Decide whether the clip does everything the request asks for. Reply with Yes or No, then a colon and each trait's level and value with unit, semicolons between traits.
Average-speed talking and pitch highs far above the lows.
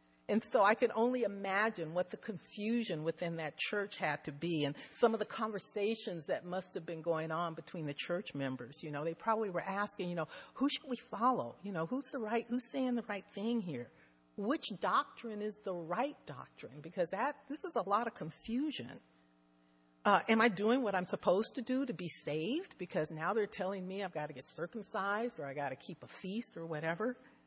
No: fast, 215 wpm; wide, 6.0 semitones